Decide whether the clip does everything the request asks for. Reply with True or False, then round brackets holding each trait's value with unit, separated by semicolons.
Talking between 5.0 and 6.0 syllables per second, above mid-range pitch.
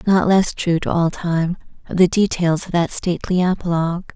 False (5.4 syllables/s; 175 Hz)